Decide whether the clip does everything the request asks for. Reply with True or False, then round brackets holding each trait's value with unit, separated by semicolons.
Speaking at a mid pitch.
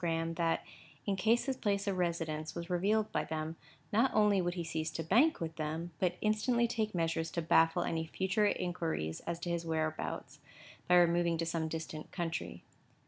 True (170 Hz)